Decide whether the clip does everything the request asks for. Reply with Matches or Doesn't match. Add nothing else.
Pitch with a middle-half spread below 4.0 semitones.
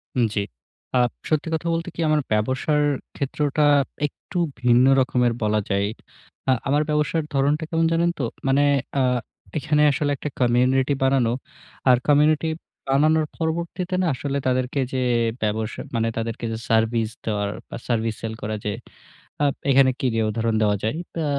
Doesn't match